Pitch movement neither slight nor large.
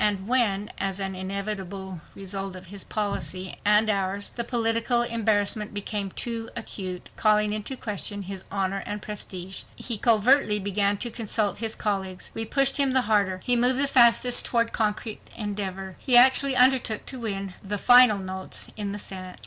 Yes: average, 3.1 semitones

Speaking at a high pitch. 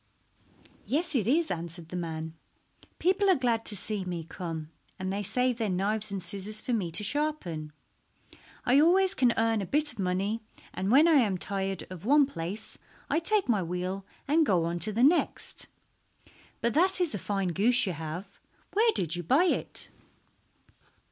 Yes: high, 210 Hz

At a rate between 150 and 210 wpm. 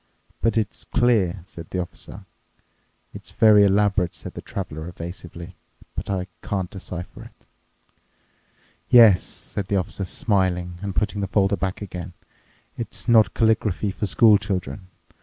No: average, 140 wpm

